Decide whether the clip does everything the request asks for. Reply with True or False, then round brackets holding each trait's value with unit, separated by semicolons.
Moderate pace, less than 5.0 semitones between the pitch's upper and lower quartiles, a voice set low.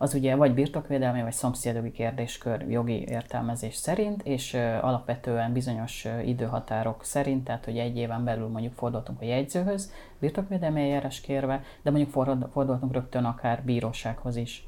True (140 wpm; 2.7 semitones; 125 Hz)